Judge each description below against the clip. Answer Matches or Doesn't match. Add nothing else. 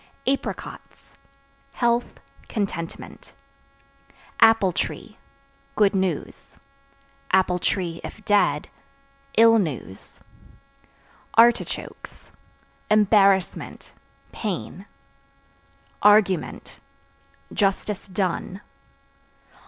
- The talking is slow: Matches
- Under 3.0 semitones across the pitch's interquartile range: Matches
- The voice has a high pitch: Matches